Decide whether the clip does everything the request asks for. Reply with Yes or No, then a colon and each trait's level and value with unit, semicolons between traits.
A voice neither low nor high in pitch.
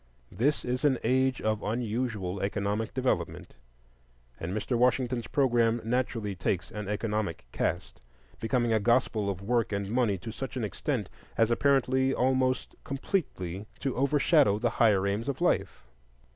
No: low, 115 Hz